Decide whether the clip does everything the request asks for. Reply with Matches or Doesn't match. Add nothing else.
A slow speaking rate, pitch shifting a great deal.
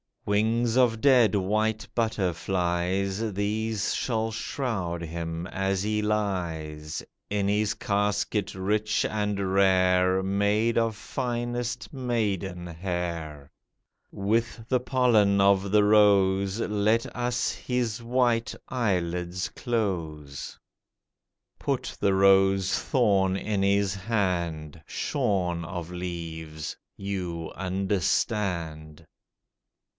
Doesn't match